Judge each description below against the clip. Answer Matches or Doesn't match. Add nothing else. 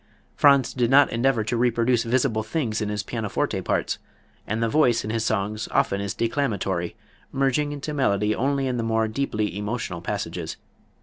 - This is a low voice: Matches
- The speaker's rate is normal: Matches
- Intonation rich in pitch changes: Doesn't match